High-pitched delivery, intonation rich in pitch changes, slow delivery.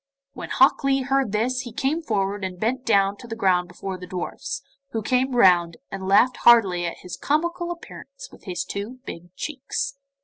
No: high, 225 Hz; wide, 6.0 semitones; average, 195 wpm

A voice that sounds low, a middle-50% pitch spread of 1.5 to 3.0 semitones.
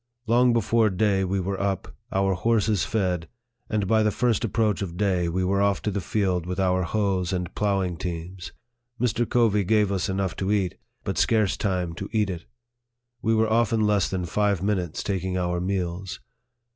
Yes: low, 100 Hz; average, 2.7 semitones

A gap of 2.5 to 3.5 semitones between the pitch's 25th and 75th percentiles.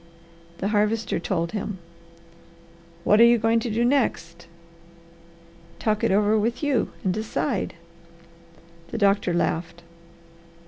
Yes: average, 3.2 semitones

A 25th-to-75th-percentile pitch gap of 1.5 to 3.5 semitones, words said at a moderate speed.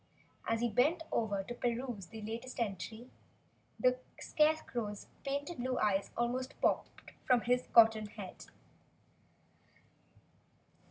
No: average, 2.9 semitones; slow, 110 wpm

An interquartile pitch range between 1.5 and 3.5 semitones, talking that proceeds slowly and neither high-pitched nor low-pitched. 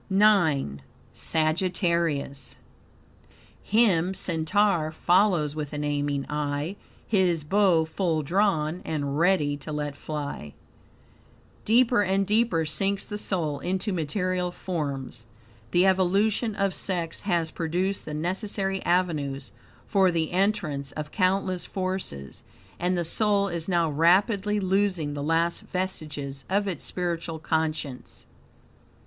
No: average, 4.2 semitones; slow, 115 wpm; medium, 175 Hz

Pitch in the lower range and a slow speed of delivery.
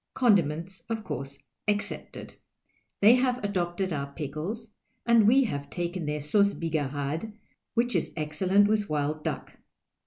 No: medium, 175 Hz; slow, 130 wpm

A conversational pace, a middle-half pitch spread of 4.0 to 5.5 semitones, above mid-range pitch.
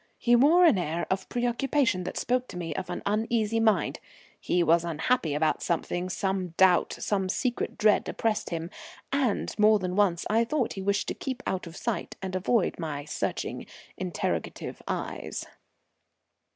Yes: average, 165 wpm; average, 4.9 semitones; high, 195 Hz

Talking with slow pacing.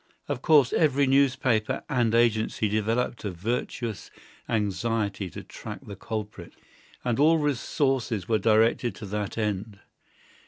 Yes: slow, 125 wpm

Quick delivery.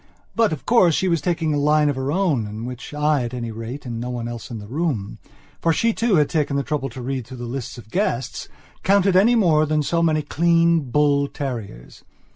Yes: fast, 220 wpm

